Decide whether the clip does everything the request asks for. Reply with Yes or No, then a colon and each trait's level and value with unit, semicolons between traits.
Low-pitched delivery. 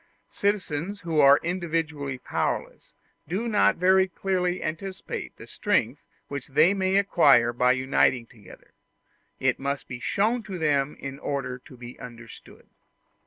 No: medium, 155 Hz